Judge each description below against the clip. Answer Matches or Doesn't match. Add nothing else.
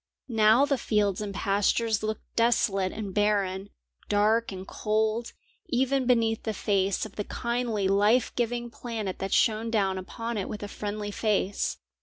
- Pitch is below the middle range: Doesn't match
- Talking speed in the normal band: Matches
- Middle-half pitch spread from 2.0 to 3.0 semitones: Matches